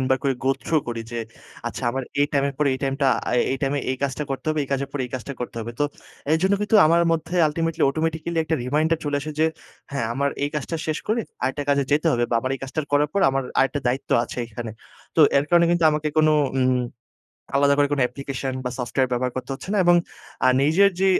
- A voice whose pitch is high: No, medium, 140 Hz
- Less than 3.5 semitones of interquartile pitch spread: Yes, average, 3.0 semitones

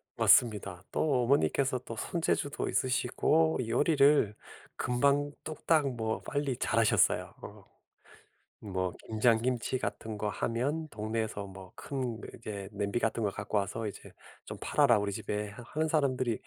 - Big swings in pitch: No, average, 4.9 semitones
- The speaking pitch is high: No, low, 115 Hz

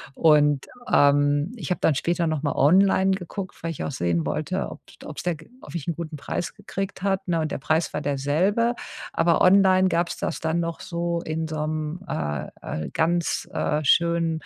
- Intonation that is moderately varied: Yes, average, 3.2 semitones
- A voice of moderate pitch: Yes, medium, 165 Hz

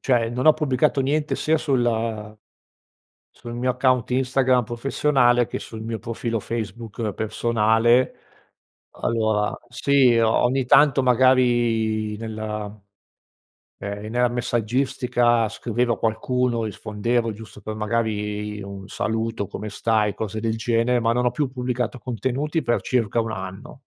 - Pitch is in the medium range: No, low, 115 Hz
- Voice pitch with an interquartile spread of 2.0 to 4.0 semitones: Yes, narrow, 2.4 semitones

